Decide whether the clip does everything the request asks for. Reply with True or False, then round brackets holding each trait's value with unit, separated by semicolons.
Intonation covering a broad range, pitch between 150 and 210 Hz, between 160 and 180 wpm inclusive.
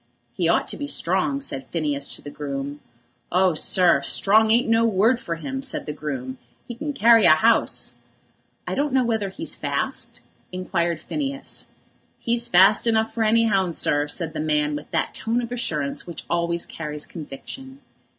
True (7.4 semitones; 190 Hz; 175 wpm)